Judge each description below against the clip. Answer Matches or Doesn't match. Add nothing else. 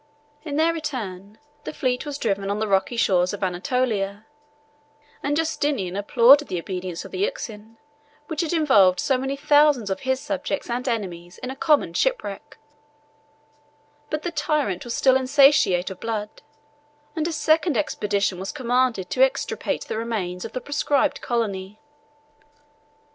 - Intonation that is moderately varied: Doesn't match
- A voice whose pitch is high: Matches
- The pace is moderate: Matches